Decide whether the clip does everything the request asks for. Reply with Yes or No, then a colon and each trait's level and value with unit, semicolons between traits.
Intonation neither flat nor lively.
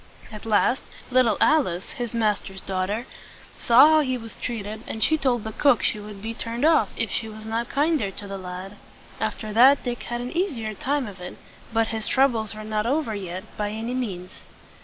Yes: average, 3.3 semitones